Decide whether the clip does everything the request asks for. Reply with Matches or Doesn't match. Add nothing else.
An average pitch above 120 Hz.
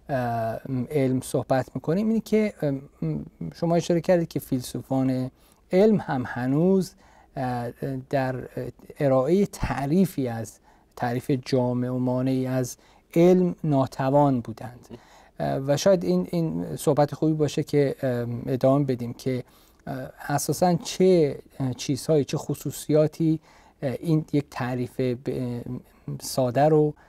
Matches